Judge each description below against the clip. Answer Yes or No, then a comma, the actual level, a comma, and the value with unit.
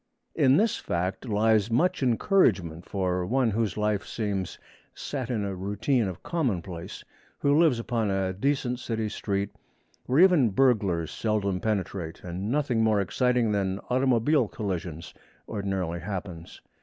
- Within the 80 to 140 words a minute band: Yes, slow, 135 wpm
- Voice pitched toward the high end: No, low, 105 Hz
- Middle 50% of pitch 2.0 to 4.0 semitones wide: No, average, 4.8 semitones